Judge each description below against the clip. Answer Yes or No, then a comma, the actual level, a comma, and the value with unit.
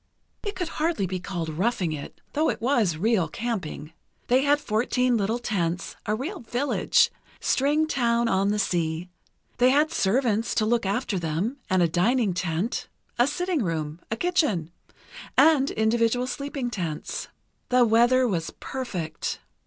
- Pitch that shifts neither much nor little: No, wide, 6.2 semitones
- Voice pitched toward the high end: Yes, high, 225 Hz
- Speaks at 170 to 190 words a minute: No, average, 150 wpm